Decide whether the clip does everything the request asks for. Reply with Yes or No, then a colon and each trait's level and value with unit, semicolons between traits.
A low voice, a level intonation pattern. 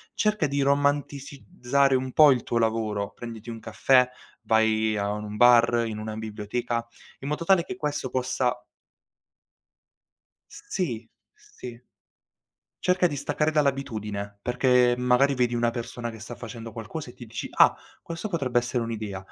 No: low, 120 Hz; average, 3.7 semitones